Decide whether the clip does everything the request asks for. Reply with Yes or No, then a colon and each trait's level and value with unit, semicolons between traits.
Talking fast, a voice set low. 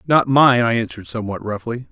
No: average, 190 wpm; low, 120 Hz